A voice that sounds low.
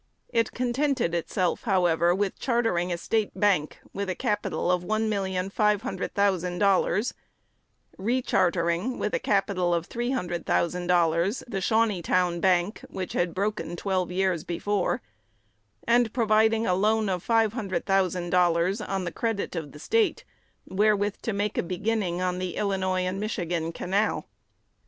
No: high, 190 Hz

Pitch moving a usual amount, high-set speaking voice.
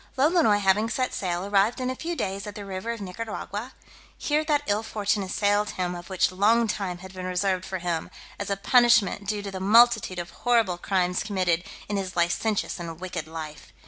Yes: average, 3.4 semitones; high, 200 Hz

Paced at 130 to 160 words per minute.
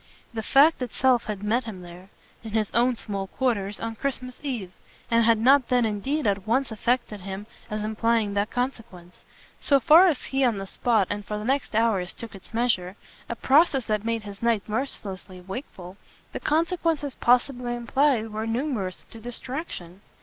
No: average, 175 wpm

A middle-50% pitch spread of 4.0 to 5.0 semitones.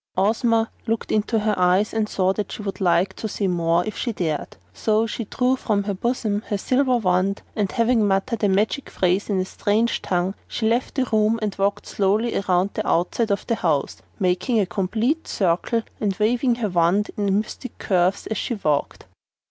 No: average, 3.2 semitones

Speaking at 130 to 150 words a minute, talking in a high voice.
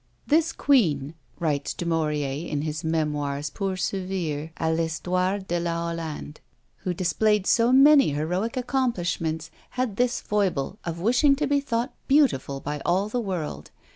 No: average, 145 wpm; medium, 175 Hz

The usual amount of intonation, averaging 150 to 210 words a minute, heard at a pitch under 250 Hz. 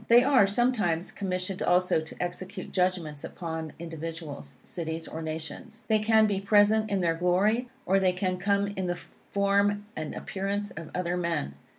Yes: average, 3.6 semitones; average, 165 wpm; medium, 185 Hz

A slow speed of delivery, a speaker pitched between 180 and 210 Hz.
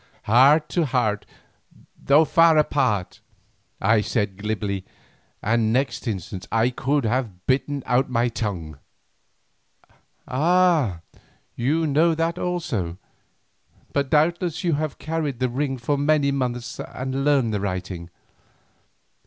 No: slow, 120 wpm; low, 130 Hz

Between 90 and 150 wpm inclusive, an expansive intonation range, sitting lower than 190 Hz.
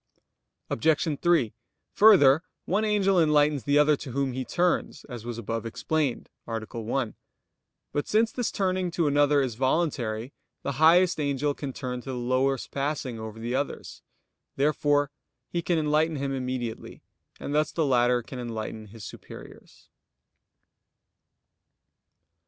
No: average, 140 wpm; average, 4.4 semitones; medium, 140 Hz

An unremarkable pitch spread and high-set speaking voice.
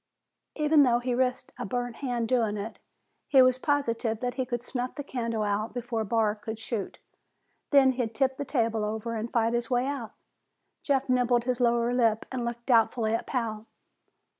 No: narrow, 2.1 semitones; high, 240 Hz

